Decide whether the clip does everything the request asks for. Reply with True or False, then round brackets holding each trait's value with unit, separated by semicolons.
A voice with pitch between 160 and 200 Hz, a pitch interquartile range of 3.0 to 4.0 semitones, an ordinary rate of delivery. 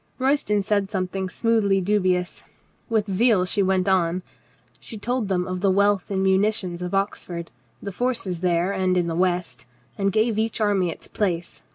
False (190 Hz; 2.5 semitones; 170 wpm)